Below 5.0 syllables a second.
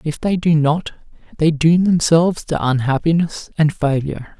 Yes: 4.8 syllables/s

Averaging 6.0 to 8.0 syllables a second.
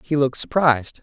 Yes: 6.5 syllables/s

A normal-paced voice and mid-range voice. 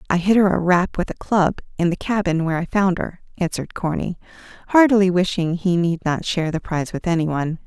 No: fast, 220 wpm; medium, 180 Hz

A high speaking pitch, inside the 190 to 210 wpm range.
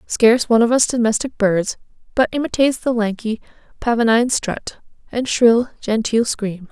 No: high, 230 Hz; average, 145 wpm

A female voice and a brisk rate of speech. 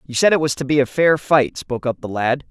No: male; fast, 310 wpm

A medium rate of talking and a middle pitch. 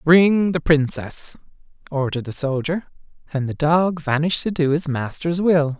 Yes: average, 155 wpm; medium, 155 Hz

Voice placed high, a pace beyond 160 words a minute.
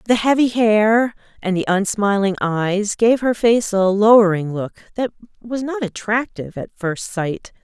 No: high, 210 Hz; average, 155 wpm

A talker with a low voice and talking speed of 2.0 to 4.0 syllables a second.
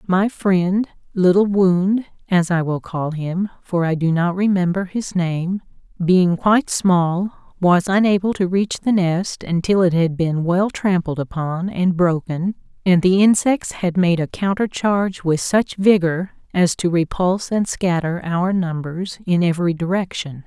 No: medium, 180 Hz; 3.6 syllables/s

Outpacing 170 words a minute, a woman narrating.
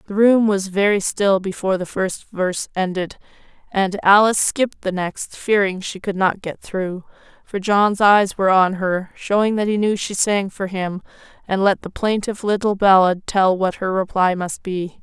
Yes: average, 190 wpm; female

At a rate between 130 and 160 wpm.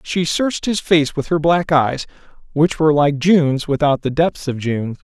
No: average, 200 wpm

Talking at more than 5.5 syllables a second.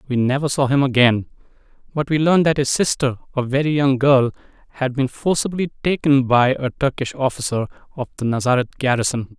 Yes: 5.8 syllables/s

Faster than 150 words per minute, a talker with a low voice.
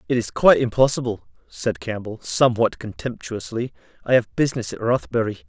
No: average, 140 wpm; low, 115 Hz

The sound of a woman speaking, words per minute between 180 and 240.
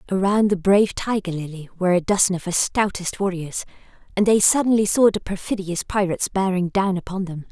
Yes: female; average, 185 wpm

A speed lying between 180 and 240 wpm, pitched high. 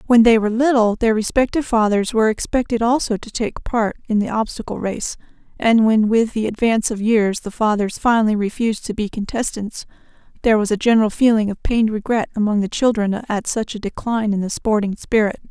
Yes: average, 195 wpm; high, 220 Hz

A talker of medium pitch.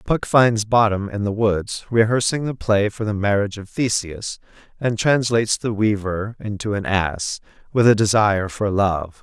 No: low, 105 Hz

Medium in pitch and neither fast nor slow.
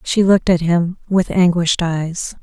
Yes: medium, 175 Hz; average, 175 wpm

